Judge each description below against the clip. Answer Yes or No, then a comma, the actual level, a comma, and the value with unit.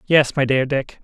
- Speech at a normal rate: No, fast, 230 wpm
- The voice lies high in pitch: No, low, 135 Hz